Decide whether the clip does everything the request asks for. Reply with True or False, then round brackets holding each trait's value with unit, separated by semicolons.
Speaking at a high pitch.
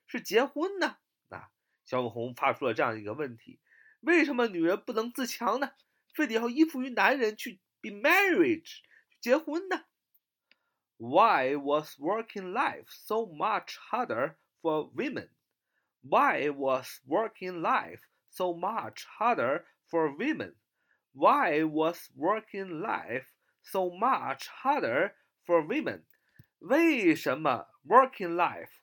True (220 Hz)